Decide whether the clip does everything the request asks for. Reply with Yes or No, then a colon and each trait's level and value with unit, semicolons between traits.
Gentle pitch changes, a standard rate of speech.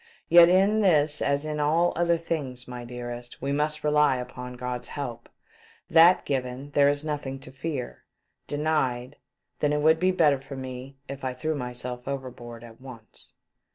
No: average, 3.4 semitones; average, 170 wpm